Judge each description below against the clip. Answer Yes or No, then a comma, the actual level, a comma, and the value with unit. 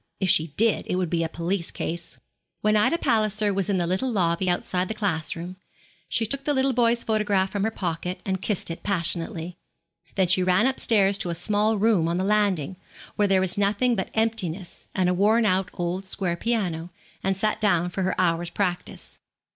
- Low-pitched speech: No, high, 190 Hz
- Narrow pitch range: No, average, 3.2 semitones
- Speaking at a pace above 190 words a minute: Yes, average, 200 wpm